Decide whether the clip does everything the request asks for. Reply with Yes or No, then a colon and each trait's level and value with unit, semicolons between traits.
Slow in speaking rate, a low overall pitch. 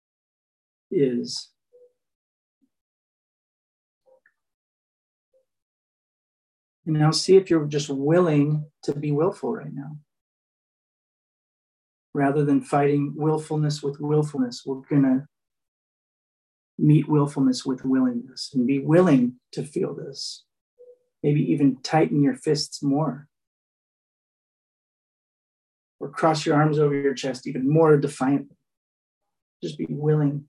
No: slow, 100 wpm; medium, 150 Hz